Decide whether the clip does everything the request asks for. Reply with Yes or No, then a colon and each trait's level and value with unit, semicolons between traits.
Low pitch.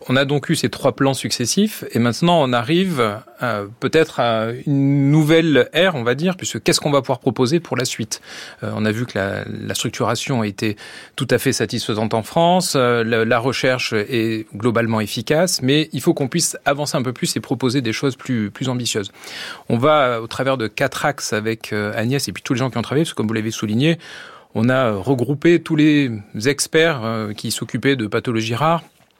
Yes: low, 130 Hz